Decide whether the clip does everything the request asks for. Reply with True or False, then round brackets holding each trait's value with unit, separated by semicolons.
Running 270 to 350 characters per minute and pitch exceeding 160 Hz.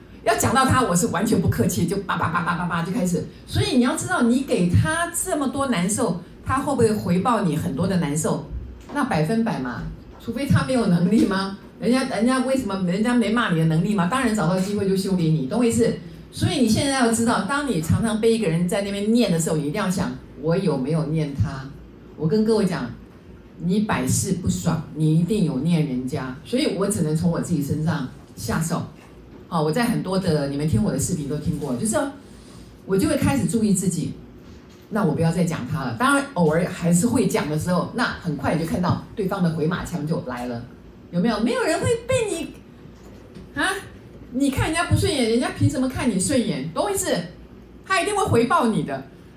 True (310 characters per minute; 190 Hz)